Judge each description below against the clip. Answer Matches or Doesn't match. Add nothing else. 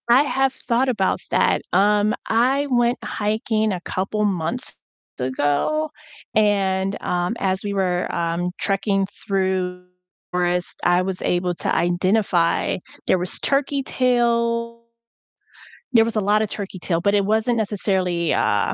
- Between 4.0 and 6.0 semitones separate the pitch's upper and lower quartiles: Matches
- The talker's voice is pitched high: Matches